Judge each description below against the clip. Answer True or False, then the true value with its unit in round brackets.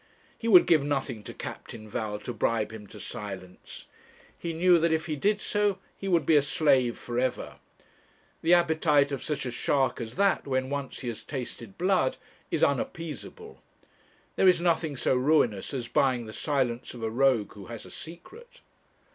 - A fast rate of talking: False (180 wpm)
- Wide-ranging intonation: True (5.9 semitones)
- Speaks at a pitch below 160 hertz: True (140 Hz)